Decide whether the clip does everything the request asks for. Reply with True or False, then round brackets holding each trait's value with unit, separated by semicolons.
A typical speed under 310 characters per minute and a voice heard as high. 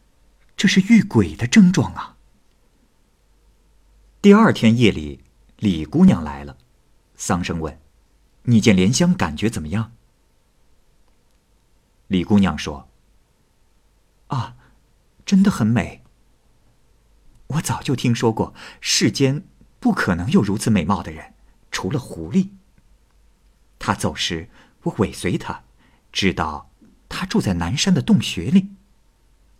False (160 characters per minute; 110 Hz)